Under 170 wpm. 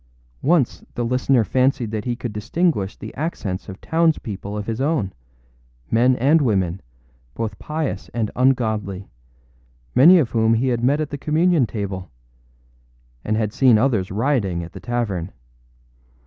Yes: average, 150 wpm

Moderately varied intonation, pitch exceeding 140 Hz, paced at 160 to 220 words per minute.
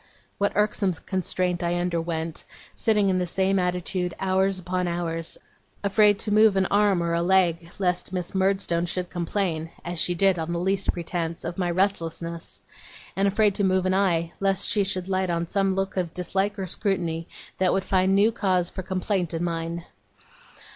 No: narrow, 2.2 semitones; medium, 185 Hz; average, 180 wpm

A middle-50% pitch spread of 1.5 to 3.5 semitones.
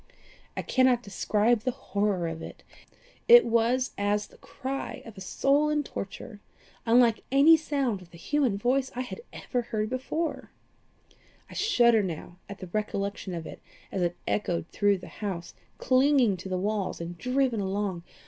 No: average, 5.0 semitones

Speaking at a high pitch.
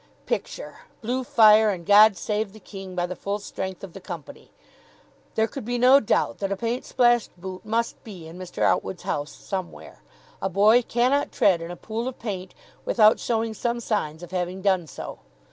Yes: high, 205 Hz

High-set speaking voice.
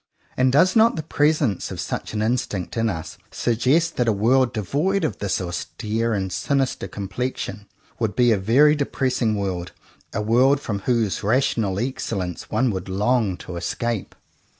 No: low, 115 Hz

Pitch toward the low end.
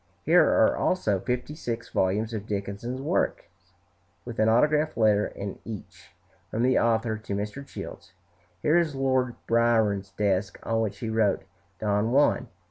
Yes: low, 115 Hz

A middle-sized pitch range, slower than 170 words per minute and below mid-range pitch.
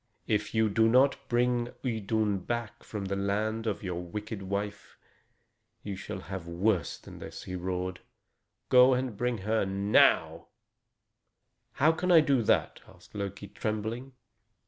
Yes: average, 3.4 semitones; average, 145 wpm; low, 105 Hz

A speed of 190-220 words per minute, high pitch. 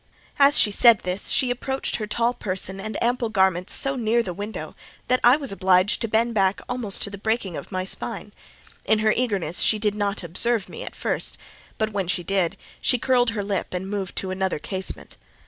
Yes: fast, 205 wpm; high, 205 Hz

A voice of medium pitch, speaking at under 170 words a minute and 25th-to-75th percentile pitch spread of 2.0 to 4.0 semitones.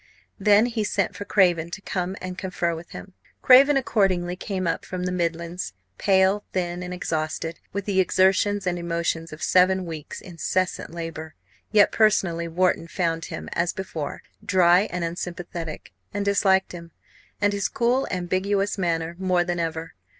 Yes: medium, 180 Hz; average, 155 wpm; narrow, 2.5 semitones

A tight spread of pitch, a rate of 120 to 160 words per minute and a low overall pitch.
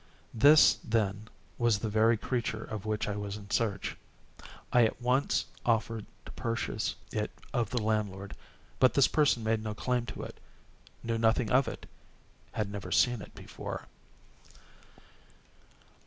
Yes: narrow, 2.2 semitones; average, 140 wpm; low, 110 Hz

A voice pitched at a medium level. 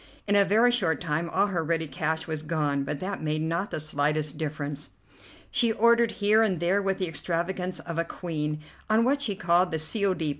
Yes: medium, 170 Hz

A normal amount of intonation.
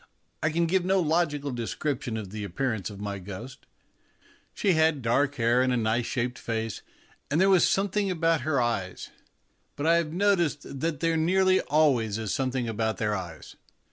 No: wide, 6.6 semitones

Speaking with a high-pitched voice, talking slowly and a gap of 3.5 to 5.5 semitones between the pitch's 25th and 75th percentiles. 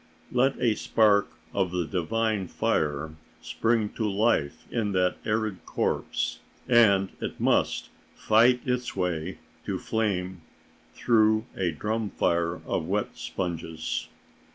No: low, 100 Hz; slow, 120 wpm; average, 3.9 semitones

